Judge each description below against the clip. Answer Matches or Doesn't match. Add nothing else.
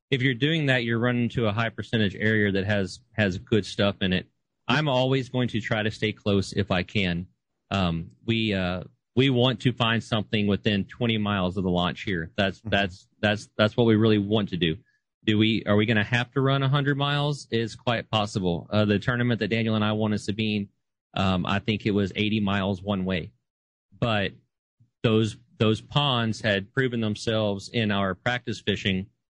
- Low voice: Matches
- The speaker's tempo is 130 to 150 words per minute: Doesn't match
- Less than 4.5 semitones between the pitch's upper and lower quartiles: Matches